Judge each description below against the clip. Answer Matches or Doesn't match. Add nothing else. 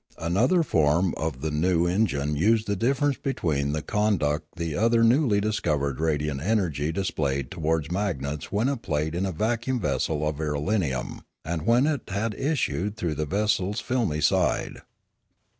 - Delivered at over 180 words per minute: Doesn't match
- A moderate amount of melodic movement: Doesn't match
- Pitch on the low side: Matches